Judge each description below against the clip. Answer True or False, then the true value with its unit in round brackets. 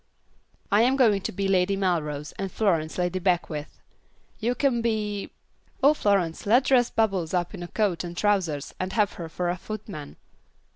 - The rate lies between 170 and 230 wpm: True (175 wpm)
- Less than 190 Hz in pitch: False (195 Hz)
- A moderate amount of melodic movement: True (3.7 semitones)